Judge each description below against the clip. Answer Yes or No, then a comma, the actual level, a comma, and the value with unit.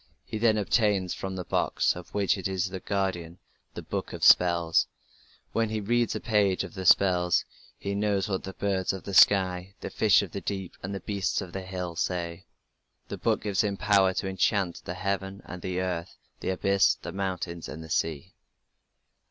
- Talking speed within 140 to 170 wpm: No, average, 195 wpm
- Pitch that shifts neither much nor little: No, narrow, 1.9 semitones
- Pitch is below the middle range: Yes, very low, 95 Hz